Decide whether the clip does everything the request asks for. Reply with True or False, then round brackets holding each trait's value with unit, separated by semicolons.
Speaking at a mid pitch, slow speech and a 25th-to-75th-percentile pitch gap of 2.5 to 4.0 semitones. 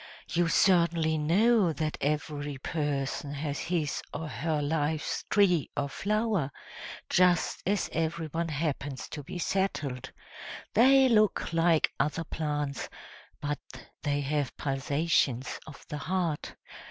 True (155 Hz; 115 wpm; 3.1 semitones)